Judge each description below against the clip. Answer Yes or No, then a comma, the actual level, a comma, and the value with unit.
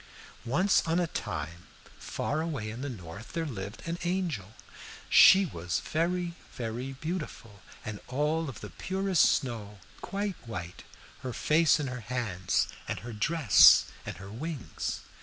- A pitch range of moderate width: No, wide, 7.7 semitones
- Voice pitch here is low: Yes, low, 130 Hz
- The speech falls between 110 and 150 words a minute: Yes, average, 145 wpm